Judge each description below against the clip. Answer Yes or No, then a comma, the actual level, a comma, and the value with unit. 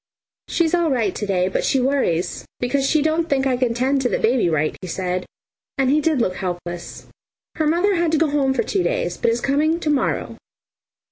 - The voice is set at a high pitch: Yes, very high, 270 Hz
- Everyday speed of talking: No, fast, 215 wpm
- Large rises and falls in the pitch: Yes, wide, 7.5 semitones